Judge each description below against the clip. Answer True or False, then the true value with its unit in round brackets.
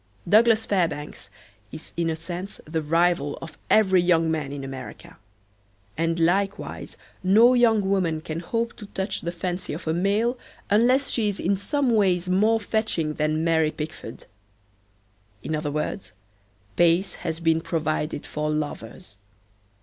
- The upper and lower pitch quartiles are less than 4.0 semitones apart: False (4.4 semitones)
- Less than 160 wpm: True (145 wpm)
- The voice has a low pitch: False (170 Hz)